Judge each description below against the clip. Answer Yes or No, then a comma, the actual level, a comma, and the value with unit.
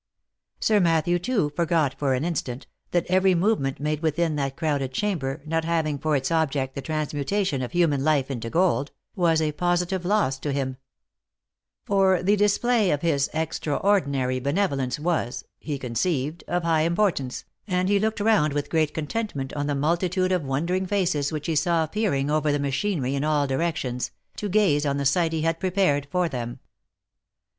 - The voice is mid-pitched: Yes, medium, 155 Hz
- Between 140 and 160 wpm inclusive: No, average, 170 wpm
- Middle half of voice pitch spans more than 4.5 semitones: No, average, 4.2 semitones